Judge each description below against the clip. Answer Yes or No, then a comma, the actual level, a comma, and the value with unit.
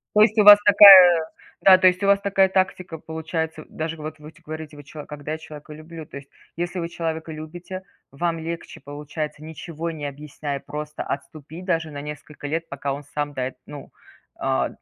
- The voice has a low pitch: No, medium, 160 Hz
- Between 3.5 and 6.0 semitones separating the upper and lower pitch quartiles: No, narrow, 2.6 semitones